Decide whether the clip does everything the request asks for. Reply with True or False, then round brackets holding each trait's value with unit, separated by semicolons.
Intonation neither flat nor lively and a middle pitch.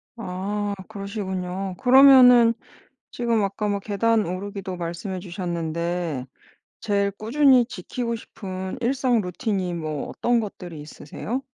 False (4.2 semitones; 200 Hz)